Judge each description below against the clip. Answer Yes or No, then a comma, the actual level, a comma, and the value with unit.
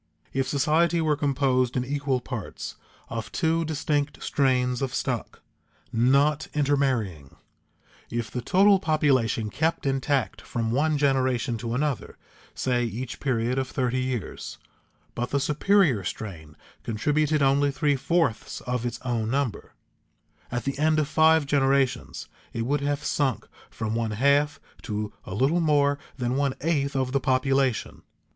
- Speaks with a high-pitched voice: No, low, 135 Hz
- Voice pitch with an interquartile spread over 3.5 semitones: No, average, 3.1 semitones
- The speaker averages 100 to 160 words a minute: Yes, average, 140 wpm